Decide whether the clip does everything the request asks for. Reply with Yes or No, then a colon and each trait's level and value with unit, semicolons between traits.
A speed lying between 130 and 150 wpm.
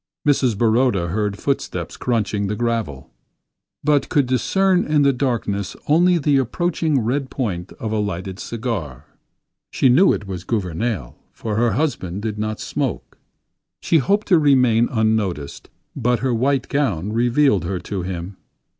Yes: average, 145 wpm